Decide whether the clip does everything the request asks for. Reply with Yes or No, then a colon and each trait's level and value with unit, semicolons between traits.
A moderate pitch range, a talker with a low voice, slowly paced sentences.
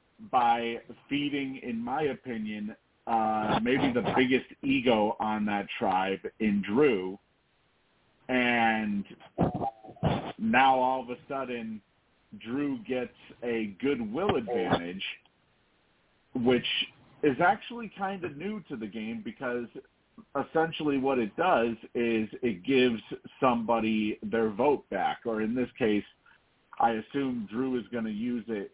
Yes: average, 4.1 semitones; low, 120 Hz; slow, 125 wpm